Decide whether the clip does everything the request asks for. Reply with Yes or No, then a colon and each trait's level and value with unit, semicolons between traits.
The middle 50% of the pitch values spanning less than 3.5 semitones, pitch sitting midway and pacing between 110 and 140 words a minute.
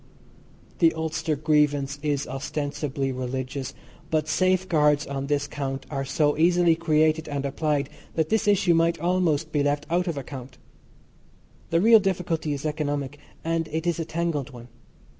No: average, 2.8 semitones; medium, 150 Hz; average, 150 wpm